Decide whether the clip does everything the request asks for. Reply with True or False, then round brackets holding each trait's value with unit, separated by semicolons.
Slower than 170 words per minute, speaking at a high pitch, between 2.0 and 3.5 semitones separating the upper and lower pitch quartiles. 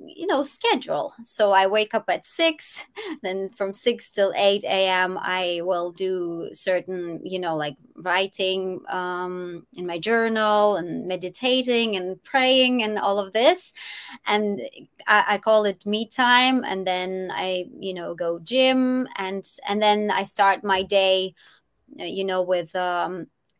False (155 wpm; 195 Hz; 3.9 semitones)